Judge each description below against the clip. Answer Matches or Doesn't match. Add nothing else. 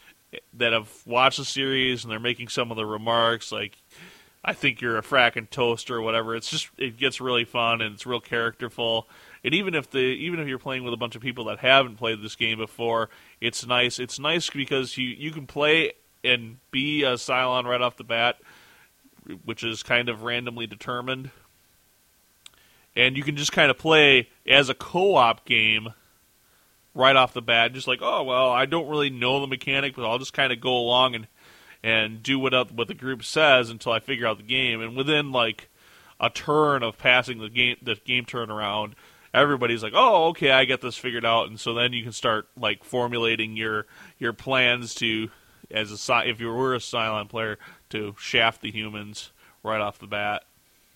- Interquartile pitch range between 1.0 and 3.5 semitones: Matches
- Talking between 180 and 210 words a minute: Matches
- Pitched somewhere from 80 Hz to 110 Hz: Doesn't match